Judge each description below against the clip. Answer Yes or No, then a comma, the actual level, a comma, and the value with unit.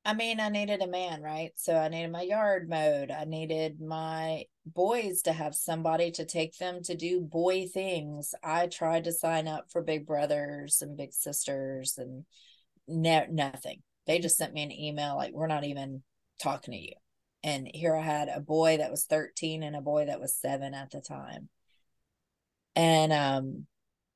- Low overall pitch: No, medium, 160 Hz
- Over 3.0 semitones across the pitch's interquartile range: No, narrow, 2.4 semitones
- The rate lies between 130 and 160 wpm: No, average, 185 wpm